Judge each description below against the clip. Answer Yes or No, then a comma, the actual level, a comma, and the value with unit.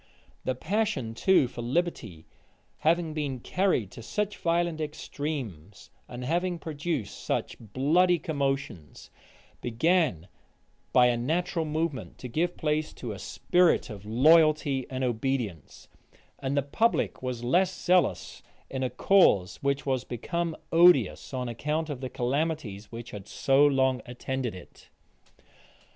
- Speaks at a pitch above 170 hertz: No, medium, 140 Hz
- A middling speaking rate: No, slow, 130 wpm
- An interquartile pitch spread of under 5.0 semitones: No, wide, 5.4 semitones